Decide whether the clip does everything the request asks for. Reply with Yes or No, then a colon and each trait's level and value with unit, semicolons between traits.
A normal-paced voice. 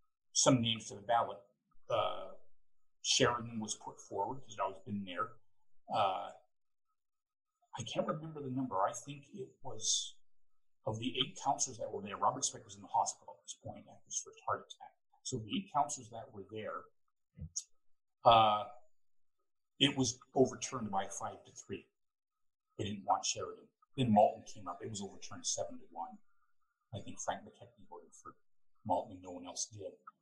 Yes: average, 175 wpm